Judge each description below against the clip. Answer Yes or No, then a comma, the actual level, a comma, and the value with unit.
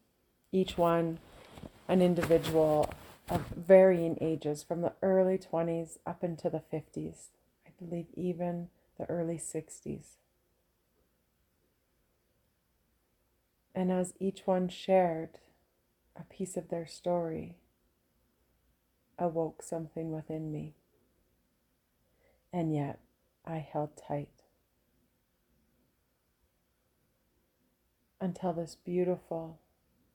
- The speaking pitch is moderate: Yes, medium, 160 Hz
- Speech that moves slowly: Yes, slow, 85 wpm